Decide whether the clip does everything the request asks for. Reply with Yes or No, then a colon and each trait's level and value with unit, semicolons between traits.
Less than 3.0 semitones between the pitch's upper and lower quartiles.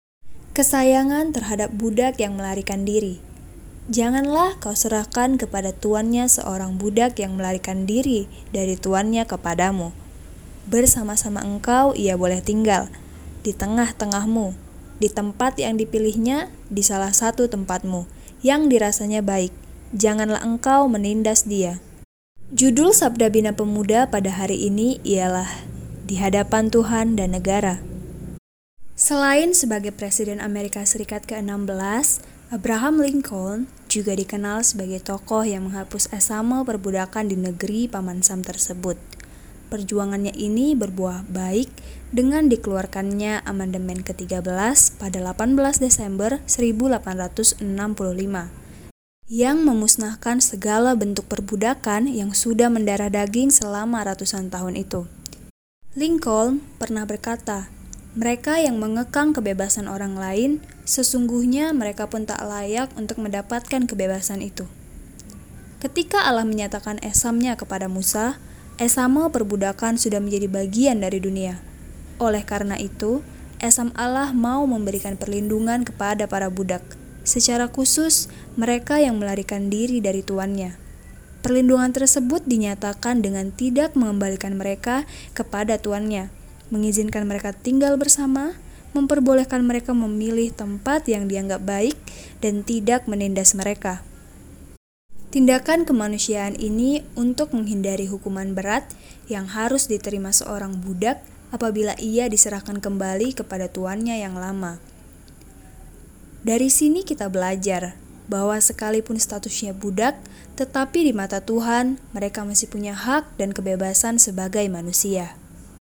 No: average, 3.5 semitones